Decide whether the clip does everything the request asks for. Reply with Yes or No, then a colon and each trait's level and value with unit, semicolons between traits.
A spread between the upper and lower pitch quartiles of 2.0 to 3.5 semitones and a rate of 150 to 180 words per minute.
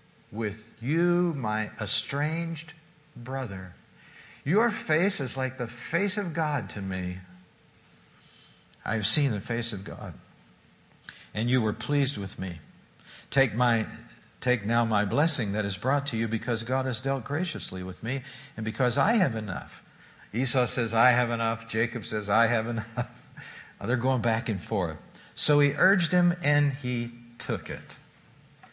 No: average, 4.5 semitones; average, 155 wpm